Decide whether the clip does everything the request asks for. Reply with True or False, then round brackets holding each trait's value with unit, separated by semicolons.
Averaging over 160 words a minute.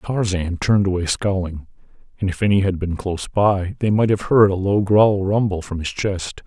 True (205 wpm)